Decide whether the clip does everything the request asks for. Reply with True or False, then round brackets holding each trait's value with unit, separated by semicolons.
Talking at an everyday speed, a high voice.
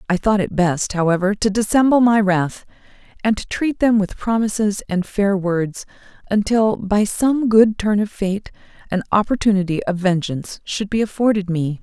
True (165 wpm; 200 Hz)